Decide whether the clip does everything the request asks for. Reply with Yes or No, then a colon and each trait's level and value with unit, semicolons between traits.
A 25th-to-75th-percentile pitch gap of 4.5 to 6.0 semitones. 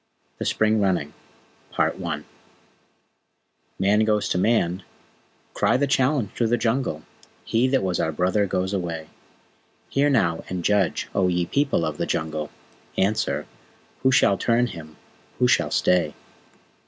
Yes: average, 5.3 semitones